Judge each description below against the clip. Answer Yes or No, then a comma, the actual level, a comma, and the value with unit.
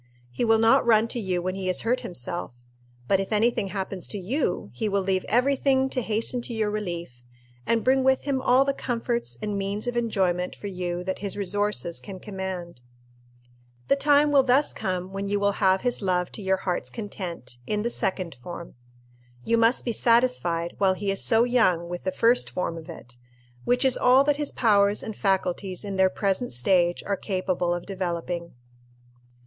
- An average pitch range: Yes, average, 4.4 semitones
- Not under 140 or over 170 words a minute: No, average, 195 wpm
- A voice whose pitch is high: Yes, high, 200 Hz